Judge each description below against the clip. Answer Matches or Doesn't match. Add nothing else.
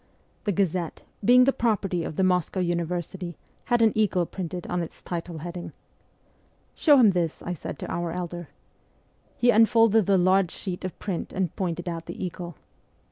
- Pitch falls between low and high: Matches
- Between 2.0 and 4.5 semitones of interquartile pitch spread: Matches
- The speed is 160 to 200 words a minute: Matches